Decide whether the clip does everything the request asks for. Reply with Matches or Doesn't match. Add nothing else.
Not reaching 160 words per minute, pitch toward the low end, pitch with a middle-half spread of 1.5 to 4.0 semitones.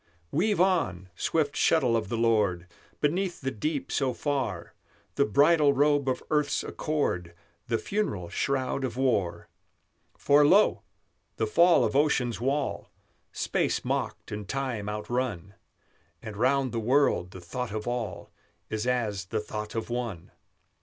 Doesn't match